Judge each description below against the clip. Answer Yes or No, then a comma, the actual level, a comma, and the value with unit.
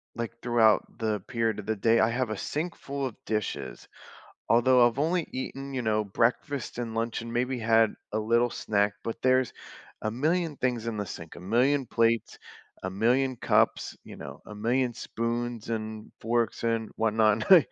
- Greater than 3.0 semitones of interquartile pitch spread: No, narrow, 2.6 semitones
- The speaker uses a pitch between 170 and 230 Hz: No, low, 115 Hz